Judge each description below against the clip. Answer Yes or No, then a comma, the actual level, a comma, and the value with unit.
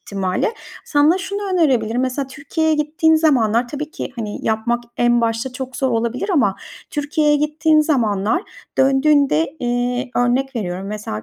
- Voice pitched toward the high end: Yes, very high, 260 Hz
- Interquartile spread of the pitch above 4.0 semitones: Yes, average, 4.7 semitones